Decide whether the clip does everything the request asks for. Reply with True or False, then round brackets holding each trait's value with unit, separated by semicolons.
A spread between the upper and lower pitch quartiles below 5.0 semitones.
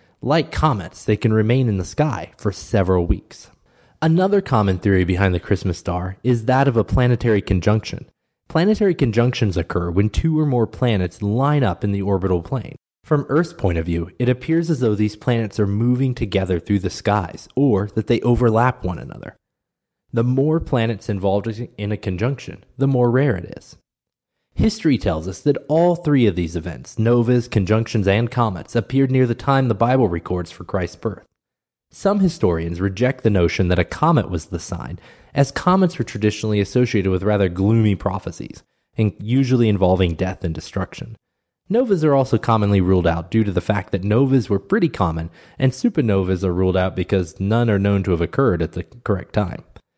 False (5.3 semitones)